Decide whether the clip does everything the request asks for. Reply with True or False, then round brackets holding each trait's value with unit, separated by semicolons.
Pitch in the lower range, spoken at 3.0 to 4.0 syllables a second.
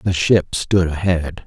True (85 Hz; 3.6 syllables/s)